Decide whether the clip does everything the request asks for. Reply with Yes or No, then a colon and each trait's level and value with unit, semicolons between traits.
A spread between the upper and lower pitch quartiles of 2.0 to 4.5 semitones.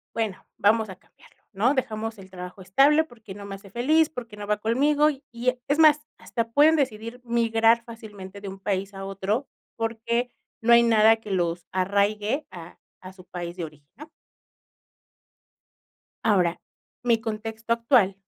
Yes: average, 3.5 semitones